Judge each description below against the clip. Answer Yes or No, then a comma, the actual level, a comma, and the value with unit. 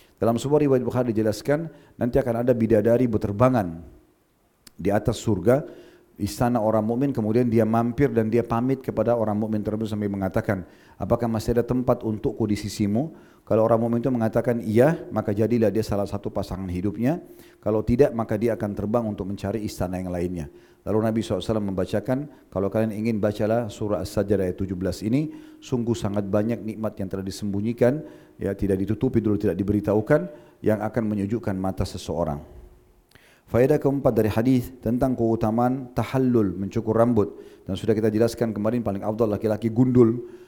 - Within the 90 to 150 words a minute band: No, fast, 160 wpm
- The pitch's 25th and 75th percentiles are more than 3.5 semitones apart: No, average, 2.7 semitones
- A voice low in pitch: Yes, low, 110 Hz